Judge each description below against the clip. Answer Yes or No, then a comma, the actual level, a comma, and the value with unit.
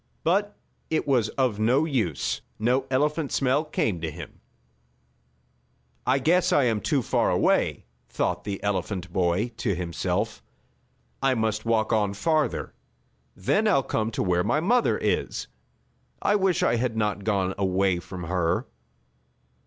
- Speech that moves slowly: No, average, 145 wpm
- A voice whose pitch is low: Yes, low, 110 Hz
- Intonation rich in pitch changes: Yes, wide, 6.4 semitones